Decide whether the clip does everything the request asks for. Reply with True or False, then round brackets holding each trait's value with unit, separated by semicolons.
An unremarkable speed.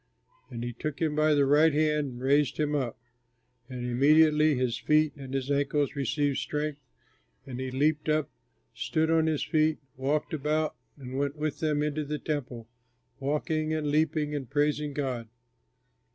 True (165 wpm)